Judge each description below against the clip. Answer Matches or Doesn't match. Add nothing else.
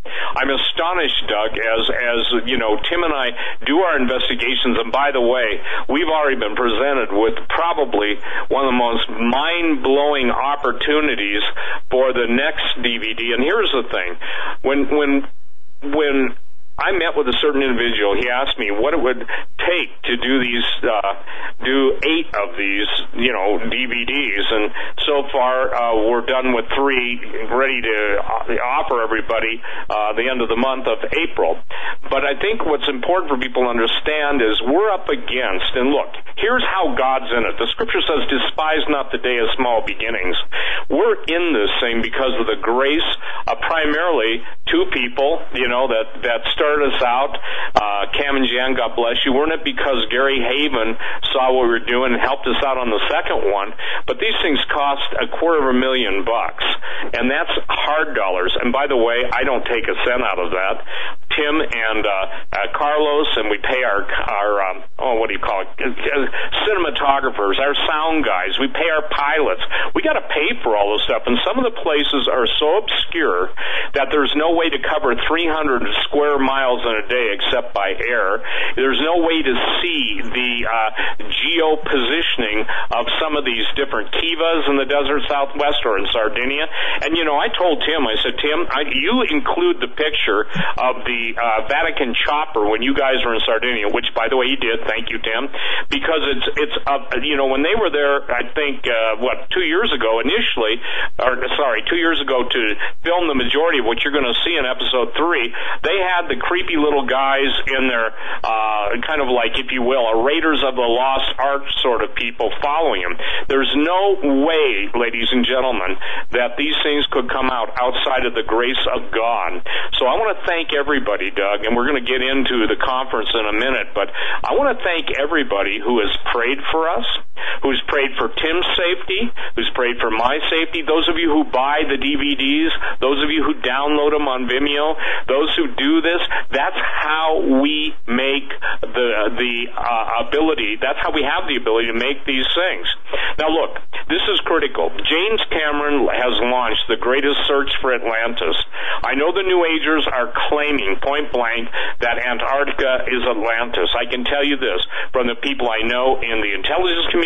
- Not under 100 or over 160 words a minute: Doesn't match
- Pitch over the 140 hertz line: Doesn't match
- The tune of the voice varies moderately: Matches